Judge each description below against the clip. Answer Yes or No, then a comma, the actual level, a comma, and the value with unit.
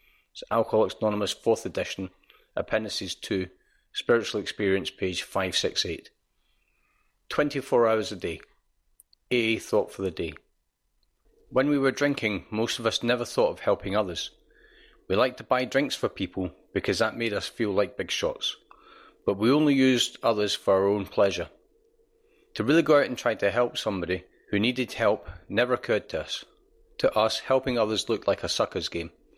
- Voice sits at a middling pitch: No, low, 125 Hz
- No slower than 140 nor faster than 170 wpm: Yes, average, 165 wpm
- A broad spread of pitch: Yes, wide, 6.1 semitones